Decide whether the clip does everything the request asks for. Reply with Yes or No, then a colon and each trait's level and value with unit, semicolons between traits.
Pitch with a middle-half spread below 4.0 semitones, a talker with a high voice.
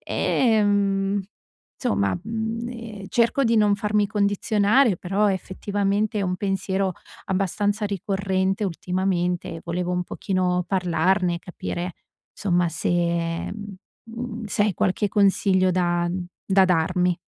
Yes: narrow, 2.5 semitones; high, 195 Hz